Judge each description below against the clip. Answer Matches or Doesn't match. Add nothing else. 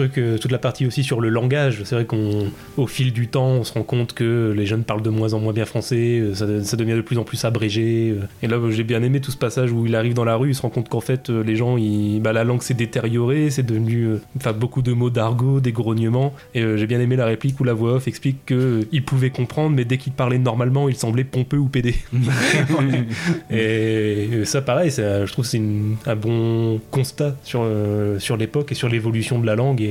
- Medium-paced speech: Doesn't match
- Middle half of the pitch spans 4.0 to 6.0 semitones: Doesn't match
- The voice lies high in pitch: Doesn't match